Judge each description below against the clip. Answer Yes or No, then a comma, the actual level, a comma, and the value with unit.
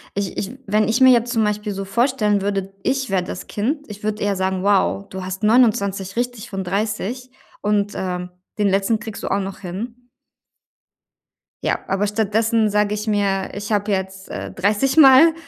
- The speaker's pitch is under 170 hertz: No, high, 205 Hz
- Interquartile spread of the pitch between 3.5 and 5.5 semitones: No, average, 2.7 semitones